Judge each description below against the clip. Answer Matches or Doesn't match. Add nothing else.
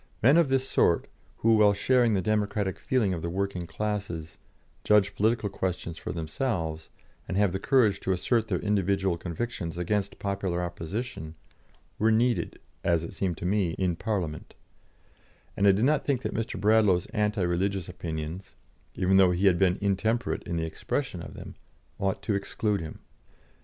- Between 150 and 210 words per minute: Matches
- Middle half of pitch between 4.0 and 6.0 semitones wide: Doesn't match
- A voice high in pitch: Doesn't match